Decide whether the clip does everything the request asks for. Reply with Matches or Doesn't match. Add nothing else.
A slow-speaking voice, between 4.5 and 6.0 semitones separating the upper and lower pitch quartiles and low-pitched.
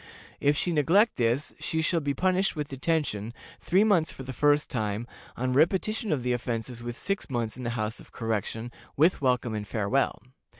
Doesn't match